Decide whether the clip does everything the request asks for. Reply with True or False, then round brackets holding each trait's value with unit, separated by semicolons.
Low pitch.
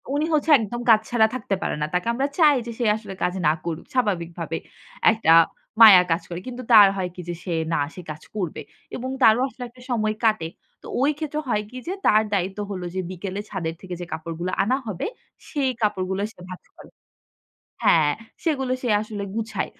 False (210 Hz)